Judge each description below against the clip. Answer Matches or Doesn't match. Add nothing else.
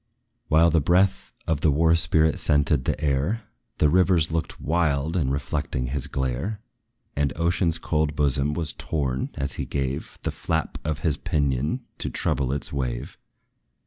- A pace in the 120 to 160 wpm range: Matches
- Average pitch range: Matches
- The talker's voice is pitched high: Doesn't match